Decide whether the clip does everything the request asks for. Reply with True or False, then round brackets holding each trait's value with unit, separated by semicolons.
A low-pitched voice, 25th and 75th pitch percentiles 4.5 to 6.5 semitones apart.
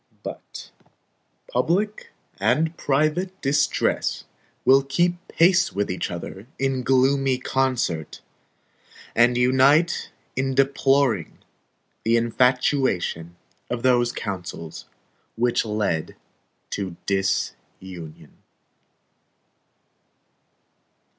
True (130 Hz; 5.5 semitones)